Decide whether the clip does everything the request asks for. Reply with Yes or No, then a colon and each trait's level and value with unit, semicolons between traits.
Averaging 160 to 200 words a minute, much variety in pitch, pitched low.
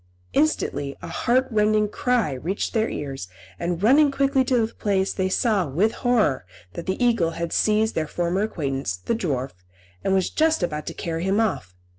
No: average, 180 wpm; wide, 6.0 semitones; high, 195 Hz